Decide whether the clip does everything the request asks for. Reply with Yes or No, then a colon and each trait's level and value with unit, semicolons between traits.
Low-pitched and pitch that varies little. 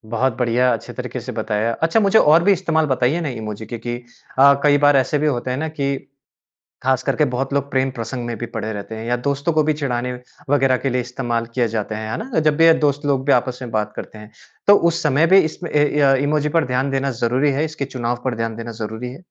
No: low, 130 Hz; average, 3.7 semitones